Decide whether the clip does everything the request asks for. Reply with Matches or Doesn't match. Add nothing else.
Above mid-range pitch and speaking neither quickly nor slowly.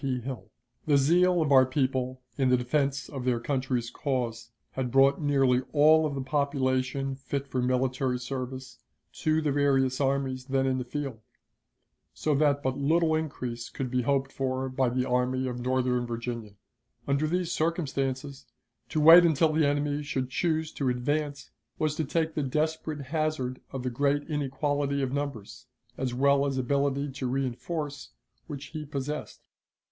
Doesn't match